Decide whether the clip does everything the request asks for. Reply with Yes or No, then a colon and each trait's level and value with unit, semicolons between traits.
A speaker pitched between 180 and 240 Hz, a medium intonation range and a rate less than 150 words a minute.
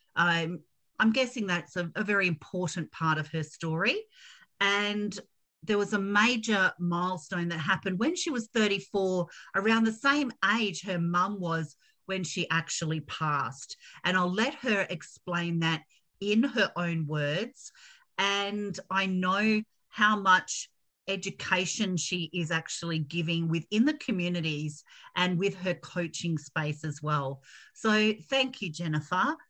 Yes: medium, 185 Hz; average, 3.9 semitones; average, 140 wpm